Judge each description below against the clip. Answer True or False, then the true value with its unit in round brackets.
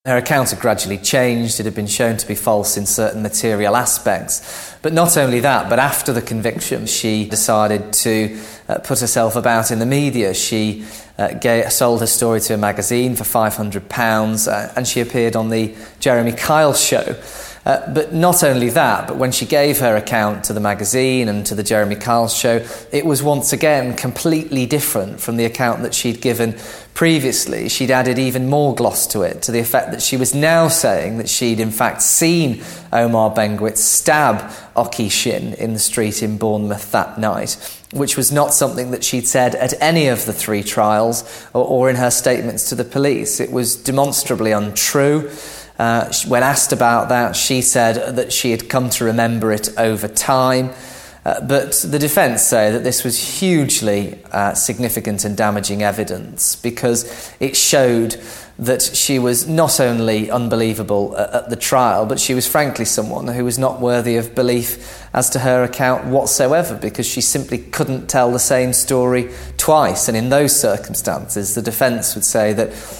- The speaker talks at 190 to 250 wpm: False (180 wpm)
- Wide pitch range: False (2.9 semitones)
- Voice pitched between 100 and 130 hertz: True (120 Hz)